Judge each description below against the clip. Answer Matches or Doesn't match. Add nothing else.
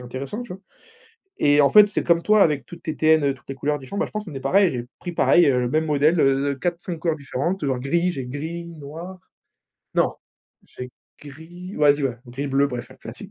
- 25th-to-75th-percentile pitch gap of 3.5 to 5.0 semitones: Matches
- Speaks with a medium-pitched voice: Matches